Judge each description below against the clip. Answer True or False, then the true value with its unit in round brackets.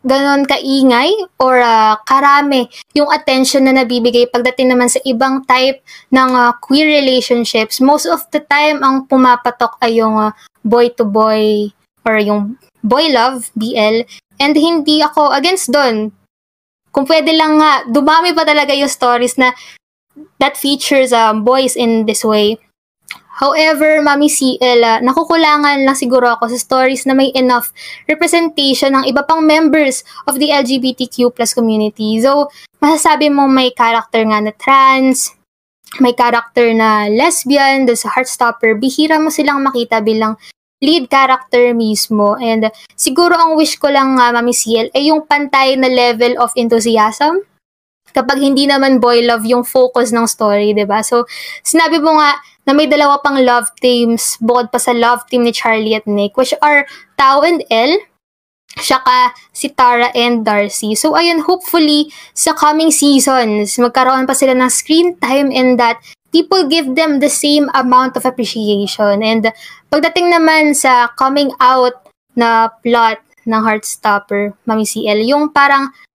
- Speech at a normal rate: True (155 wpm)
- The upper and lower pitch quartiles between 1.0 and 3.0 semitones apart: False (3.7 semitones)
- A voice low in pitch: False (260 Hz)